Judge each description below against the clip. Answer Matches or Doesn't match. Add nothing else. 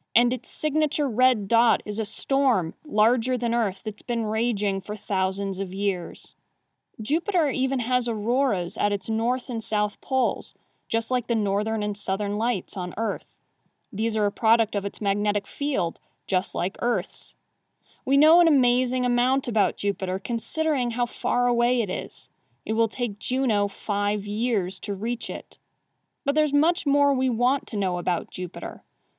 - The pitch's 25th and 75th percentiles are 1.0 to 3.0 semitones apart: Doesn't match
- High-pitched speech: Matches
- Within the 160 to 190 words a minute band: Matches